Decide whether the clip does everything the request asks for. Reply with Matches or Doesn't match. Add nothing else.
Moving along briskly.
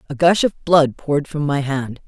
Matches